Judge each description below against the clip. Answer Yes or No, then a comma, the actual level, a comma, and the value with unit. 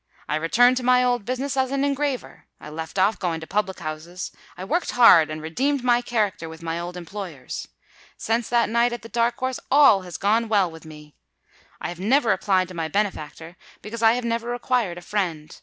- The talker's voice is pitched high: Yes, high, 210 Hz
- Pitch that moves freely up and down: Yes, wide, 6.2 semitones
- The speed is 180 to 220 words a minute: Yes, average, 195 wpm